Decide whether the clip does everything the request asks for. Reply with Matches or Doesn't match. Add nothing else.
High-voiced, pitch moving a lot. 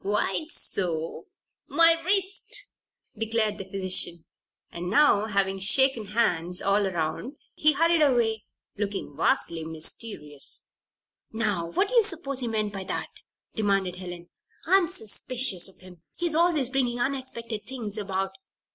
Matches